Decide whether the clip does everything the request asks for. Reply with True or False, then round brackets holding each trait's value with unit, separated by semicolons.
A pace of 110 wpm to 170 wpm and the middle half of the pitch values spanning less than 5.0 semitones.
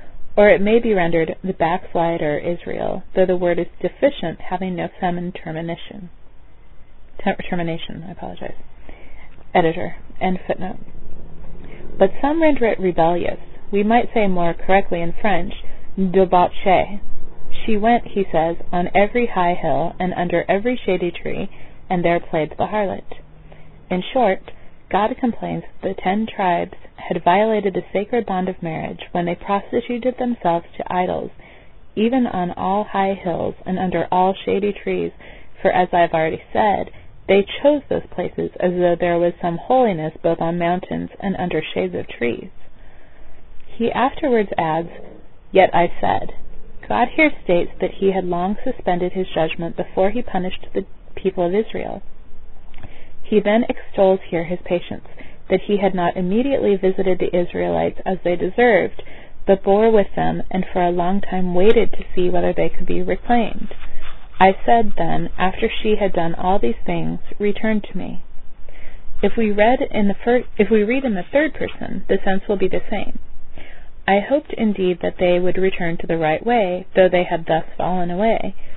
True (165 wpm; 3.5 semitones)